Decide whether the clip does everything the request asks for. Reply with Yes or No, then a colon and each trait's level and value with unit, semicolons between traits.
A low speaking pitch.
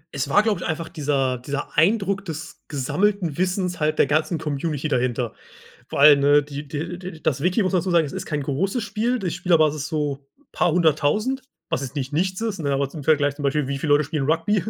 No: medium, 155 Hz